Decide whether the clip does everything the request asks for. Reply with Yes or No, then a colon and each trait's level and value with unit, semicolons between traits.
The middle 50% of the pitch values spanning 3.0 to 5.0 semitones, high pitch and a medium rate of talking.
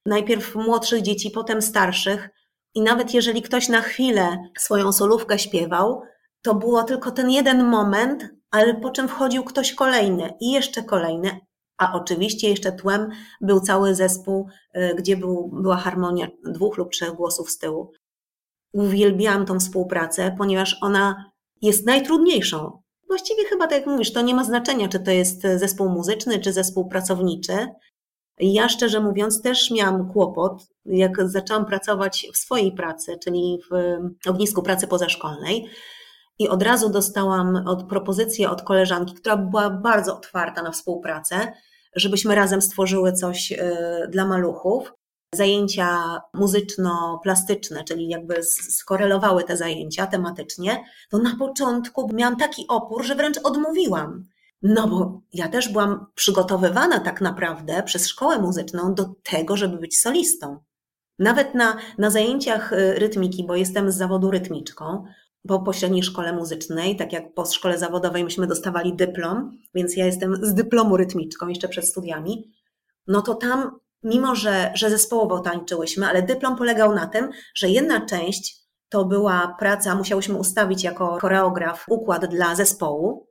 Yes: average, 3.5 semitones; high, 195 Hz; average, 145 wpm